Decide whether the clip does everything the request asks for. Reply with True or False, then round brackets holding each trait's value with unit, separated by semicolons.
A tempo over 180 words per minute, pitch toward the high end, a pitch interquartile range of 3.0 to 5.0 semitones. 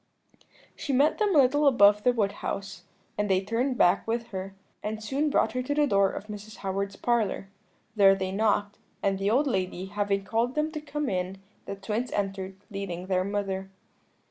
True (195 wpm; 205 Hz; 4.3 semitones)